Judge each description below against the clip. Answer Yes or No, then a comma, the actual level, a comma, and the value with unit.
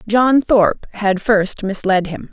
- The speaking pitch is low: No, high, 205 Hz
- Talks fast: No, average, 155 wpm